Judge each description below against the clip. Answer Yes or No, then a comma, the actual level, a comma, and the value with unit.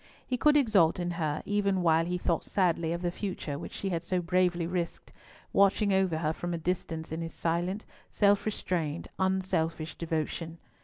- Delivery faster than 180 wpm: No, average, 175 wpm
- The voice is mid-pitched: Yes, medium, 175 Hz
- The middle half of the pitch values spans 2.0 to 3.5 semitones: Yes, narrow, 2.6 semitones